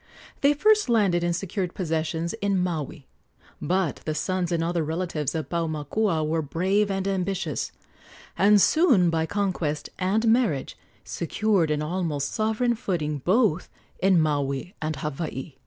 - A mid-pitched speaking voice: Yes, medium, 175 Hz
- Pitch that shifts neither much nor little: Yes, average, 4.1 semitones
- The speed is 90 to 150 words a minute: Yes, average, 140 wpm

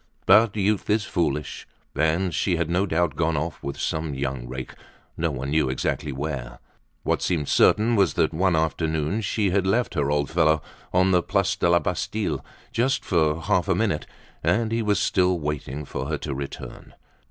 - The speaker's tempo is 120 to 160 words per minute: No, average, 185 wpm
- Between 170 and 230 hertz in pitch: No, very low, 85 Hz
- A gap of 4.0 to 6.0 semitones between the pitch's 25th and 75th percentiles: Yes, average, 4.6 semitones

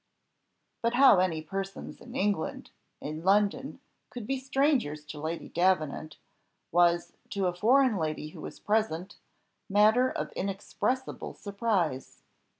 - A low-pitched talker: No, high, 195 Hz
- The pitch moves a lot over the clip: Yes, wide, 5.9 semitones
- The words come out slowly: Yes, slow, 125 wpm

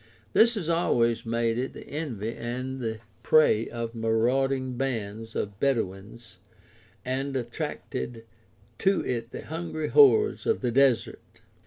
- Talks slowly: Yes, slow, 130 wpm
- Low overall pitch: Yes, low, 120 Hz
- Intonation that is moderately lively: Yes, average, 3.4 semitones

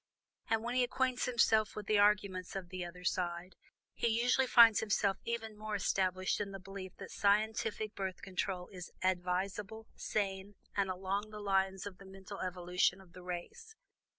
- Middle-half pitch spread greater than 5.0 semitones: No, narrow, 2.6 semitones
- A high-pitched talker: Yes, high, 195 Hz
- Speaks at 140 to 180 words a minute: Yes, average, 170 wpm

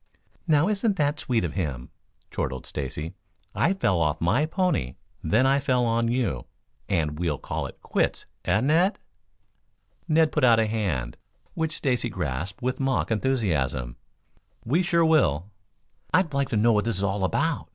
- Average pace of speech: Yes, average, 160 wpm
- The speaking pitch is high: No, low, 115 Hz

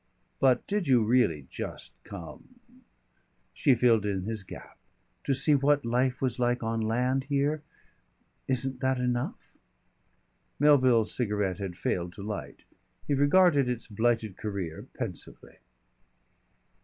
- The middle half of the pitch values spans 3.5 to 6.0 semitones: Yes, average, 4.0 semitones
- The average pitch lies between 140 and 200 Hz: No, low, 125 Hz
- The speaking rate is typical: No, slow, 130 wpm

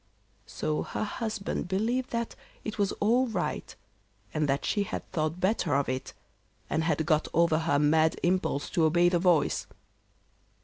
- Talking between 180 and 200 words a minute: No, average, 160 wpm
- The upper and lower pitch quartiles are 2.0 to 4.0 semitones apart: No, average, 4.8 semitones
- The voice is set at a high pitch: No, medium, 175 Hz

